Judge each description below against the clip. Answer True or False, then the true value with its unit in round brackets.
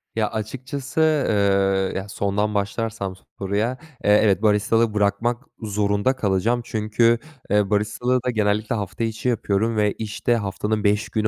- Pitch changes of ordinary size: False (2.1 semitones)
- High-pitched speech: False (105 Hz)